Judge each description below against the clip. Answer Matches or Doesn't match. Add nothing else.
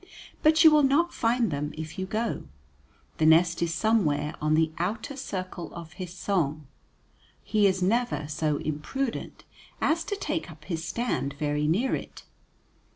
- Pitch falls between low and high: Matches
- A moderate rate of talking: Matches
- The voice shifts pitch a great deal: Matches